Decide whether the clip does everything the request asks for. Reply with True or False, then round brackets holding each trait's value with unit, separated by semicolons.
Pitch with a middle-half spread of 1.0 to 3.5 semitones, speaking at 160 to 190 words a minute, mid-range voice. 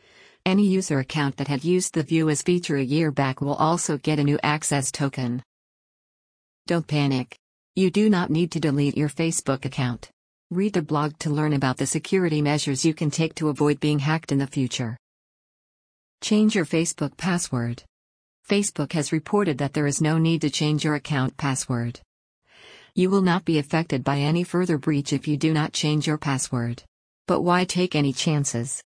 True (2.9 semitones; 180 wpm; 150 Hz)